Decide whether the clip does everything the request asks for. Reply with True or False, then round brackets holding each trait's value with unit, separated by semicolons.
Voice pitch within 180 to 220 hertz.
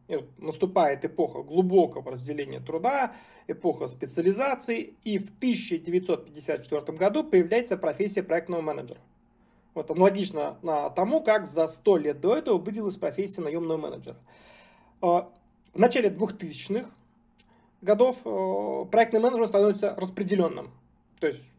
True (190 Hz)